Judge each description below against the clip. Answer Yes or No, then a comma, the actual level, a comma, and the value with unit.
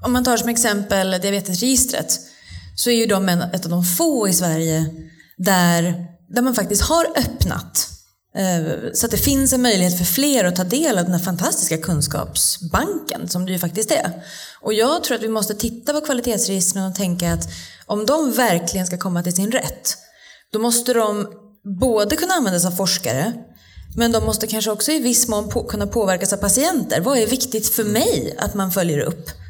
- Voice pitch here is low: No, high, 210 Hz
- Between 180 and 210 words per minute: Yes, average, 190 wpm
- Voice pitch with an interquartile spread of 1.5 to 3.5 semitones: No, average, 5.0 semitones